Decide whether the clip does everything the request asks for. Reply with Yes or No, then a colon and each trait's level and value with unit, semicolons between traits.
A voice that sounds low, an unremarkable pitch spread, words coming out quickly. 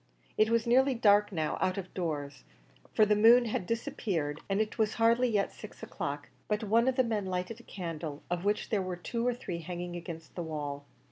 No: high, 200 Hz; average, 4.9 semitones; fast, 210 wpm